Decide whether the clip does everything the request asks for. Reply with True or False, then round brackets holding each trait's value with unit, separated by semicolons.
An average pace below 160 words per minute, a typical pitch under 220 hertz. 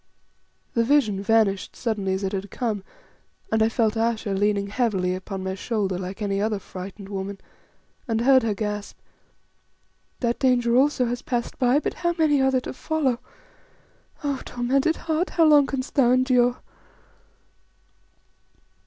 False (150 wpm; 230 Hz)